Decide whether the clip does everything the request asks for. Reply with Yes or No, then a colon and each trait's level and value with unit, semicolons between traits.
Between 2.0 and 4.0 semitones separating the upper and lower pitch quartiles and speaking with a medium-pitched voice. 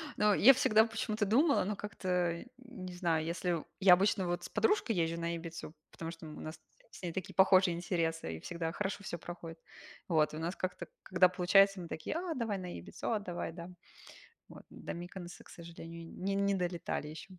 Yes: average, 3.0 semitones; medium, 180 Hz